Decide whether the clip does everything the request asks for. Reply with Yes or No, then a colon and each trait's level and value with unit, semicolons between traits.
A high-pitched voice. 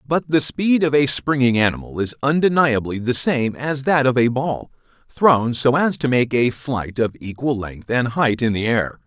No: low, 130 Hz